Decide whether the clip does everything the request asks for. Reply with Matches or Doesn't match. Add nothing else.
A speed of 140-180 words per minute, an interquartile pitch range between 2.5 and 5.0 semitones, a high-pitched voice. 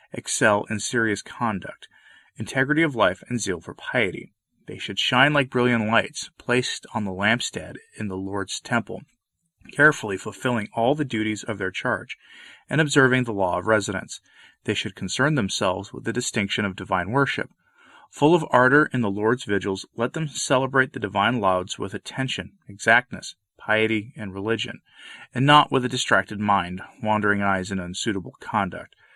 Doesn't match